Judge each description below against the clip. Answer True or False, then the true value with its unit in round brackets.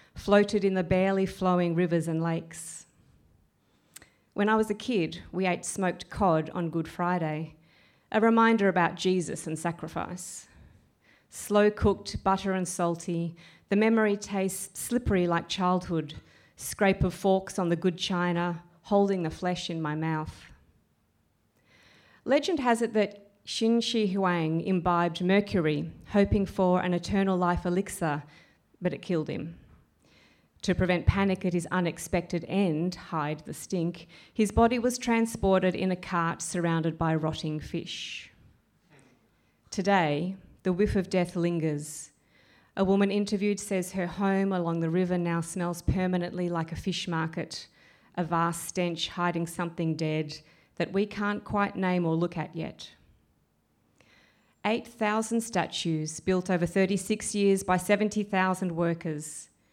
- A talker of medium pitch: True (180 Hz)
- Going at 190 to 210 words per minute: False (135 wpm)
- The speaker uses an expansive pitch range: False (2.9 semitones)